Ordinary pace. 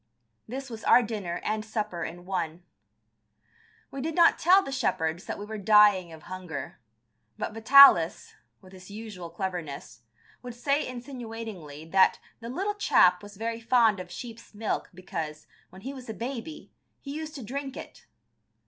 Yes: average, 160 wpm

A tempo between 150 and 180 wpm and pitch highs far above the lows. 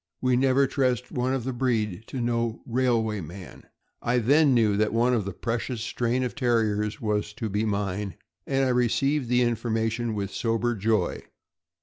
No: average, 175 wpm; average, 2.8 semitones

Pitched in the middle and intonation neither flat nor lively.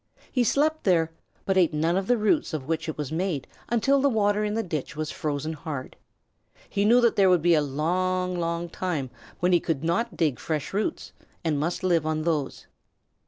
Yes: medium, 170 Hz; average, 4.5 semitones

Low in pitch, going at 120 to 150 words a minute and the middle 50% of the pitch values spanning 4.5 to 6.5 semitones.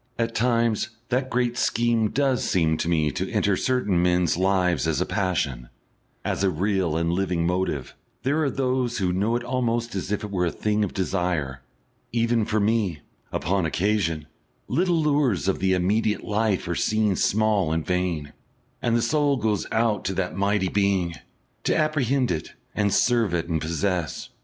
No: low, 100 Hz; average, 175 wpm; average, 4.8 semitones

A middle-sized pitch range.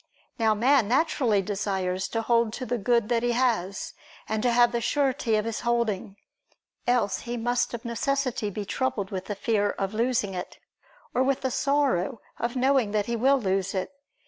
Yes: average, 3.4 semitones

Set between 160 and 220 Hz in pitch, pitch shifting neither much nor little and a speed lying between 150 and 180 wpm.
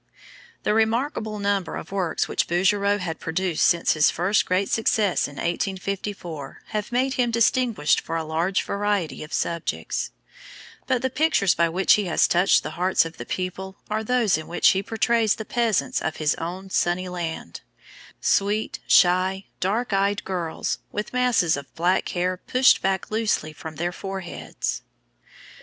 Yes: high, 190 Hz; average, 3.7 semitones; average, 160 wpm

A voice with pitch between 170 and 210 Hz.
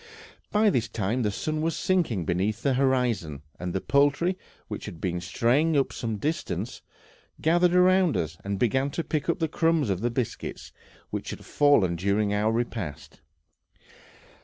No: low, 125 Hz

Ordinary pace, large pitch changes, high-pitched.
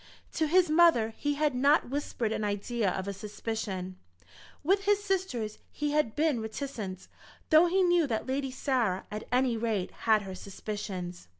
Yes: average, 165 wpm; wide, 6.4 semitones; high, 240 Hz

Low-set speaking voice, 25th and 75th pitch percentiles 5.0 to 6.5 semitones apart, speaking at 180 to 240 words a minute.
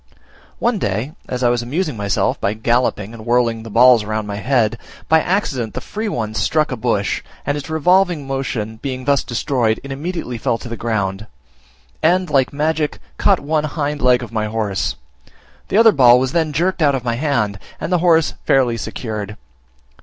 Yes: low, 125 Hz; wide, 5.4 semitones; average, 185 wpm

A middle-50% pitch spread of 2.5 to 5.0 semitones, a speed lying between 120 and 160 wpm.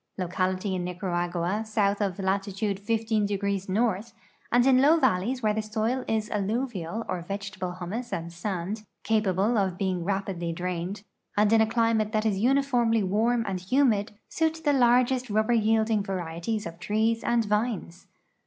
Yes: average, 3.4 semitones; average, 155 wpm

